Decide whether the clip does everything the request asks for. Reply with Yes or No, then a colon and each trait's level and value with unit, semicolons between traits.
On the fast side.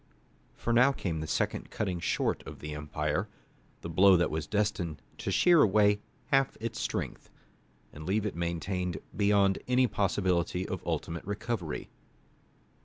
No: average, 145 wpm